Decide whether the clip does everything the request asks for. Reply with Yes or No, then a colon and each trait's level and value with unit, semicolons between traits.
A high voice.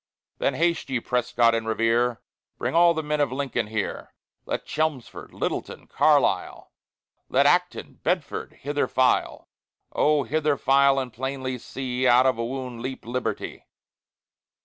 No: low, 130 Hz